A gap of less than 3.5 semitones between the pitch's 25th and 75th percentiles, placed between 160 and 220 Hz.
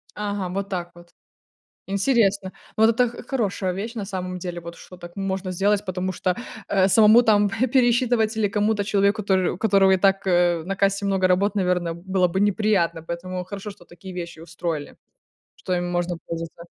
Yes: narrow, 2.6 semitones; high, 190 Hz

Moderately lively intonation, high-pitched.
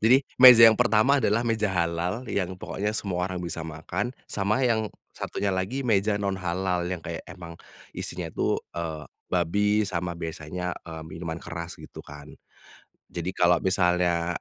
No: average, 3.8 semitones; very low, 90 Hz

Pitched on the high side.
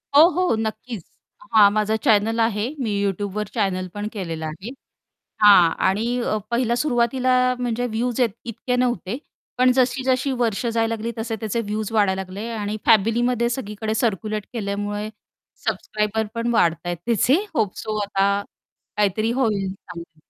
Yes: high, 220 Hz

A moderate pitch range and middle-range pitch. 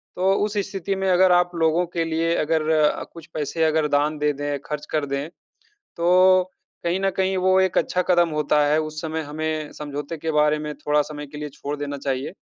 Yes: average, 3.1 semitones; medium, 155 Hz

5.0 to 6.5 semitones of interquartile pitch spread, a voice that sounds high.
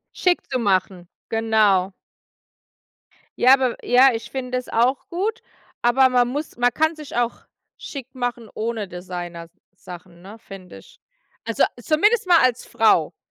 Yes: wide, 5.5 semitones; high, 240 Hz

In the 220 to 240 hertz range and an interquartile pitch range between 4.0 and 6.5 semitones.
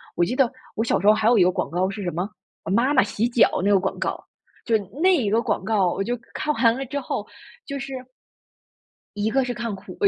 Yes: high, 225 Hz; average, 4.5 semitones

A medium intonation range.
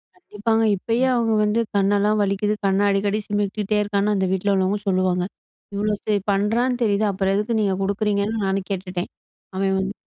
No: narrow, 1.6 semitones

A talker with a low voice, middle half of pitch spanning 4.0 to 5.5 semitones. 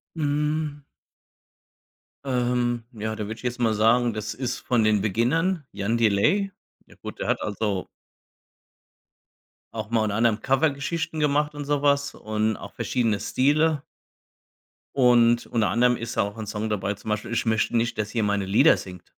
Yes: low, 120 Hz; average, 4.7 semitones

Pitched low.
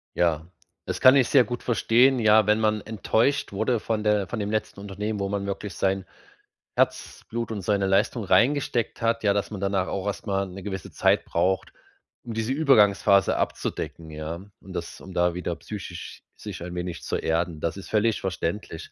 Yes: low, 100 Hz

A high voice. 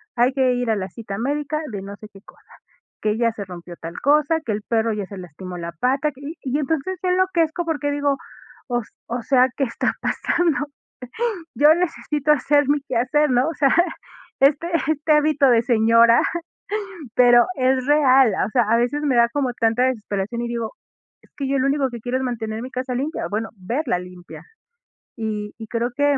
Yes: very high, 250 Hz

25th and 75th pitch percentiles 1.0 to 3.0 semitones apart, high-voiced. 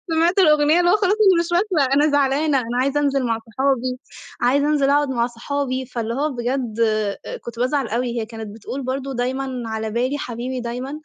No: average, 3.4 semitones; very high, 265 Hz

